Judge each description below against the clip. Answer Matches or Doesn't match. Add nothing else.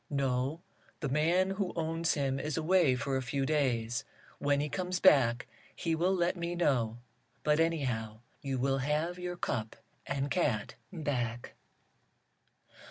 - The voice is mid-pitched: Matches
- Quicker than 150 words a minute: Doesn't match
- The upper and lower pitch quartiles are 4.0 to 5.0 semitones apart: Matches